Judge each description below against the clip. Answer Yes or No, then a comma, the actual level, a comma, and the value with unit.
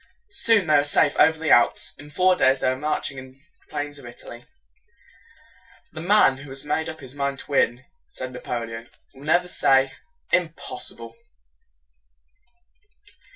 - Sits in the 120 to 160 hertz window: Yes, medium, 140 Hz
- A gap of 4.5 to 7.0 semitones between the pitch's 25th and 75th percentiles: No, average, 3.4 semitones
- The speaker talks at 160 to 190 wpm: Yes, average, 165 wpm